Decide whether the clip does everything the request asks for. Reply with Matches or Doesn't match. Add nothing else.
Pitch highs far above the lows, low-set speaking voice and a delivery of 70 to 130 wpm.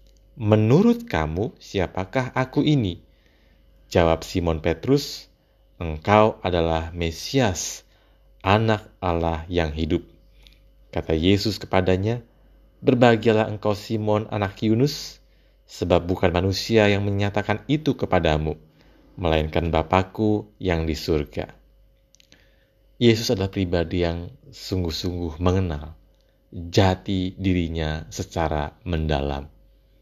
Doesn't match